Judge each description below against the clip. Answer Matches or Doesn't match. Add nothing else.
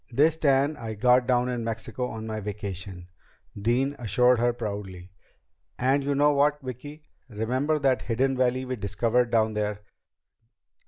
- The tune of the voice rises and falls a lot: Doesn't match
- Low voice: Matches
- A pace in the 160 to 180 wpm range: Doesn't match